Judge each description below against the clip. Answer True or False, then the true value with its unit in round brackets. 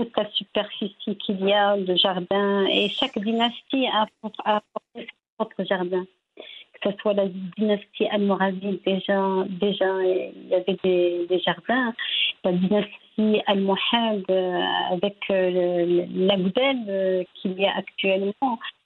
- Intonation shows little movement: True (2.2 semitones)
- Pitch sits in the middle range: False (200 Hz)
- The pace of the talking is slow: True (130 wpm)